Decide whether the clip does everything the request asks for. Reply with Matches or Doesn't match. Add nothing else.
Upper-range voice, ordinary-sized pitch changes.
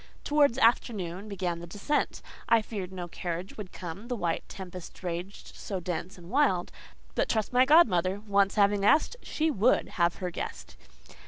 Matches